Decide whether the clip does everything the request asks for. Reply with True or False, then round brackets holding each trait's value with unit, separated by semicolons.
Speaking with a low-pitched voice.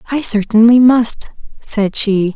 False (225 Hz)